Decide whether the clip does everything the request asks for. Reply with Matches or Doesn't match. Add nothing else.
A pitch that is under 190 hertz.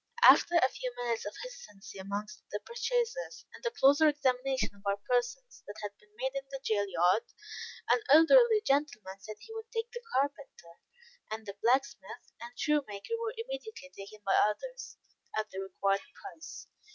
Doesn't match